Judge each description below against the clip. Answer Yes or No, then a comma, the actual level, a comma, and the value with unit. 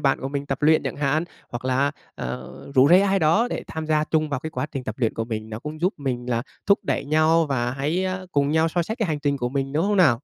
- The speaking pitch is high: No, medium, 145 Hz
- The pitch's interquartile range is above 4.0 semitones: No, average, 3.7 semitones